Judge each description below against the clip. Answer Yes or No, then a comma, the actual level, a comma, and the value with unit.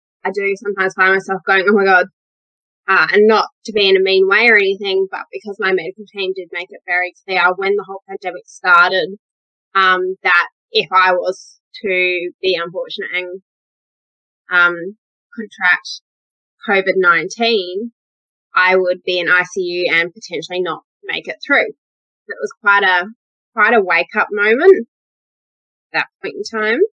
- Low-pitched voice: No, high, 195 Hz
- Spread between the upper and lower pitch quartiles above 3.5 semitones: Yes, average, 4.1 semitones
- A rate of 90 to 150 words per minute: No, average, 160 wpm